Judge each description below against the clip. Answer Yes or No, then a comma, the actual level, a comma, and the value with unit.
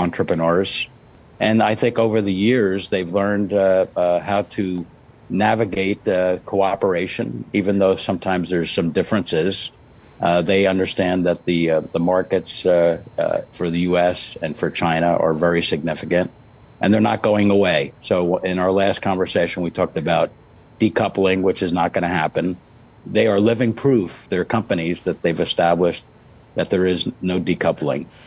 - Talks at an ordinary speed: Yes, average, 160 wpm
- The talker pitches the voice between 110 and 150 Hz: No, very low, 95 Hz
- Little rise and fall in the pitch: No, average, 3.2 semitones